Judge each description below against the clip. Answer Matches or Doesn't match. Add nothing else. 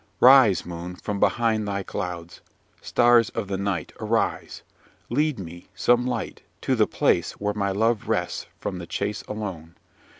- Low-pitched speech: Matches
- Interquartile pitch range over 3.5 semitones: Matches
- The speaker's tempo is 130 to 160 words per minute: Matches